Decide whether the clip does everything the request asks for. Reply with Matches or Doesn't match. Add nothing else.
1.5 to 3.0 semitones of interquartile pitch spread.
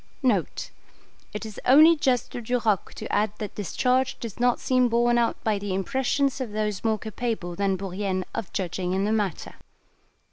Doesn't match